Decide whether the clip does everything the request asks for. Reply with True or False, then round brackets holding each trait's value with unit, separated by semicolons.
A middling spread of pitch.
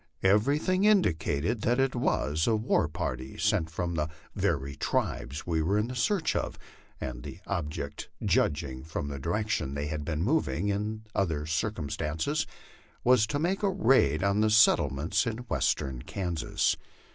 False (6.7 semitones)